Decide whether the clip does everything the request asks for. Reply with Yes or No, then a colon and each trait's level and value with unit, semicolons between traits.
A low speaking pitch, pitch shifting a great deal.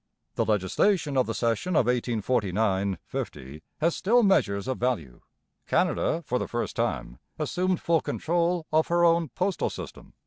Yes: low, 130 Hz; wide, 8.4 semitones